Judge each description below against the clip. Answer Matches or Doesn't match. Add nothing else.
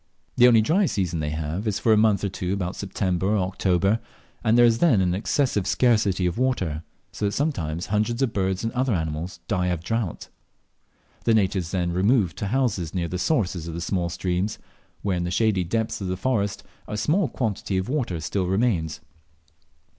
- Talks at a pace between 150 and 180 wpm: Doesn't match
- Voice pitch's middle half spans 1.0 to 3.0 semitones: Doesn't match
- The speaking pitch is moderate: Doesn't match